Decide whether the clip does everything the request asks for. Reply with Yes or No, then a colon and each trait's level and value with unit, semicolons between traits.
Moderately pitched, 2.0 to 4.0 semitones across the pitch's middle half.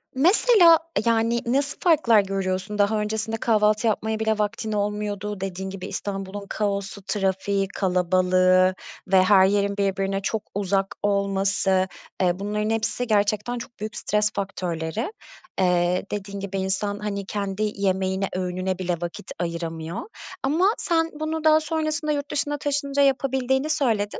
No: high, 205 Hz; average, 3.4 semitones